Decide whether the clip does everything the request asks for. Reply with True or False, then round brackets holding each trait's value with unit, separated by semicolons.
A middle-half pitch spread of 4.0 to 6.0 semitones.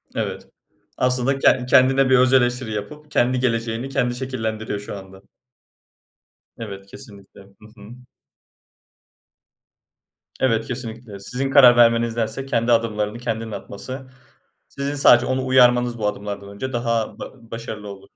False (3.2 semitones)